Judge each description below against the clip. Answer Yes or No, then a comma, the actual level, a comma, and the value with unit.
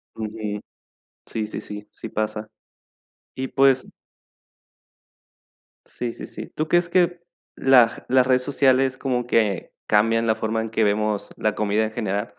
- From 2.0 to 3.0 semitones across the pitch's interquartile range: No, average, 3.6 semitones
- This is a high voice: No, low, 115 Hz